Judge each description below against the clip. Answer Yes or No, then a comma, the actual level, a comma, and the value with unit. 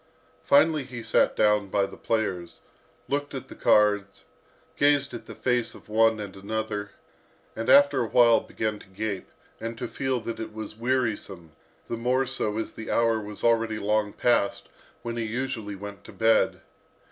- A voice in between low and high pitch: No, low, 110 Hz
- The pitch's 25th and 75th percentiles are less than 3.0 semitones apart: Yes, narrow, 2.6 semitones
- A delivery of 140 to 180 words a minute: Yes, average, 170 wpm